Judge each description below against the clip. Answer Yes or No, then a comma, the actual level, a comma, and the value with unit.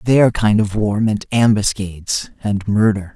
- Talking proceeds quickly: No, average, 150 wpm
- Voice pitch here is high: No, low, 105 Hz